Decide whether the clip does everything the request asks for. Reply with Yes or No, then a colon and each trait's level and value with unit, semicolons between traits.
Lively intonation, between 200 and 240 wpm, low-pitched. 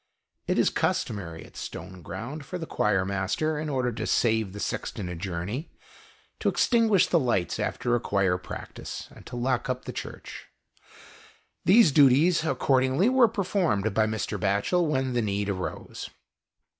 No: wide, 7.8 semitones; average, 155 wpm; low, 125 Hz